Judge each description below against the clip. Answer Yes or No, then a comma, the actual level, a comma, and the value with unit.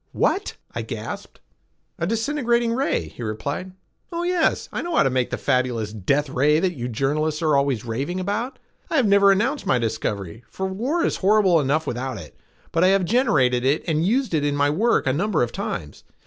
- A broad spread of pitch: Yes, wide, 8.9 semitones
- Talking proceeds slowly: No, average, 200 wpm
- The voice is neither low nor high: Yes, medium, 155 Hz